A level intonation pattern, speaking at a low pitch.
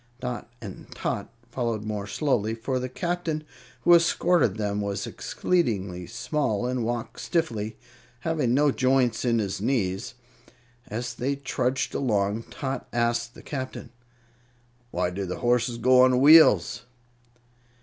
No: average, 3.8 semitones; low, 120 Hz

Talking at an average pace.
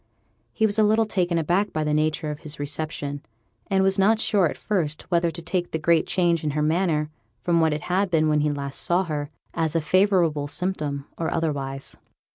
No: fast, 210 wpm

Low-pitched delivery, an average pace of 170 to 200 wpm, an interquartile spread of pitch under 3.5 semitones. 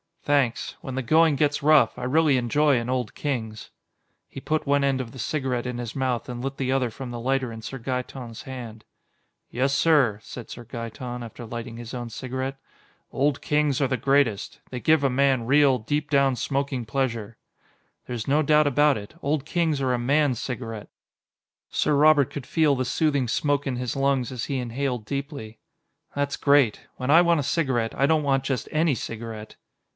Yes: low, 130 Hz; average, 190 wpm; average, 2.9 semitones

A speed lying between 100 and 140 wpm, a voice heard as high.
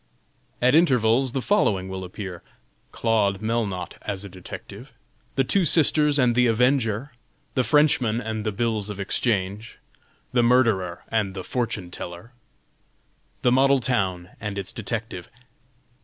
No: slow, 135 wpm; low, 115 Hz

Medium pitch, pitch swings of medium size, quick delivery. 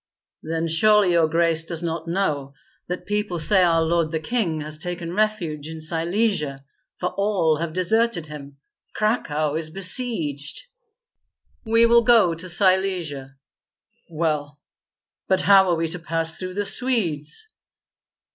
No: medium, 170 Hz; average, 3.9 semitones; slow, 135 wpm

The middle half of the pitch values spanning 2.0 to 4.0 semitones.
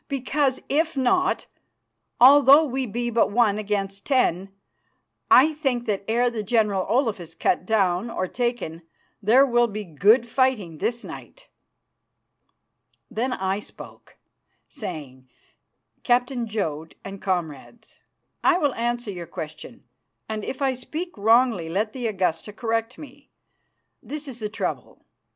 No: average, 4.7 semitones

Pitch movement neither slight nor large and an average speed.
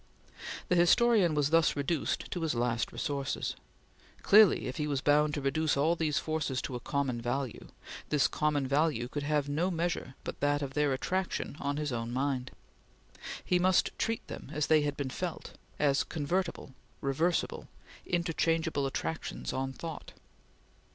Yes: average, 3.1 semitones; average, 160 wpm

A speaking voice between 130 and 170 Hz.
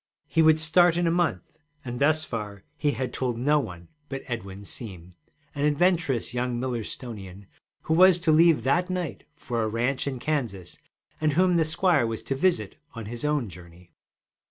Yes: low, 135 Hz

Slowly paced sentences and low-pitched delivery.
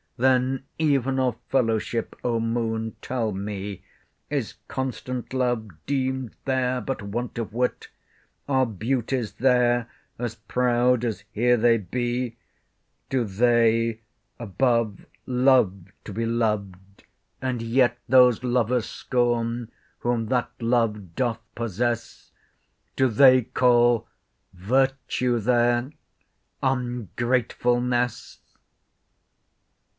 Yes: slow, 95 wpm; low, 120 Hz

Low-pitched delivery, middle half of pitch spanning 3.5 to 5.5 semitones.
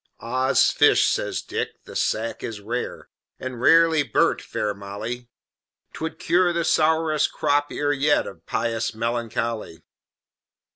Yes: low, 125 Hz; average, 5.2 semitones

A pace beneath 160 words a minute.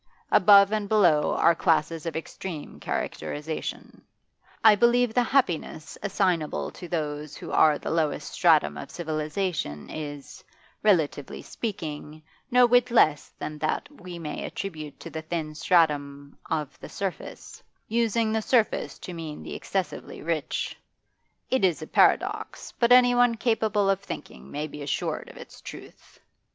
Yes: average, 140 wpm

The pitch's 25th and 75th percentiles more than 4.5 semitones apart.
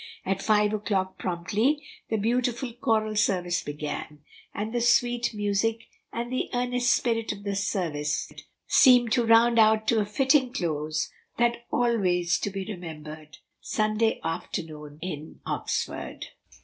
Yes: average, 5.1 semitones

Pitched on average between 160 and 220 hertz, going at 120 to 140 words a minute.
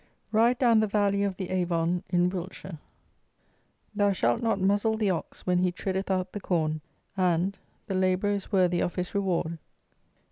No: medium, 185 Hz; average, 170 wpm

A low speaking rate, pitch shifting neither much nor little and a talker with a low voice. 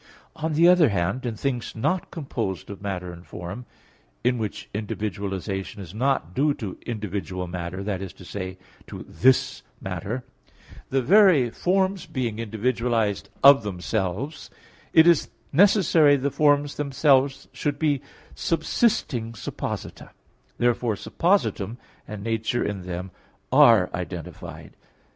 No: slow, 125 wpm; wide, 6.7 semitones; low, 115 Hz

